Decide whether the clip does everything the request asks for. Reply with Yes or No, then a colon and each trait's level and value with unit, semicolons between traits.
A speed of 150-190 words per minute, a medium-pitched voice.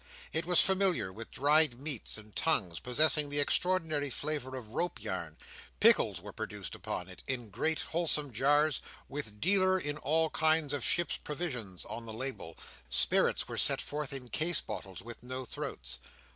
Yes: average, 165 wpm; medium, 145 Hz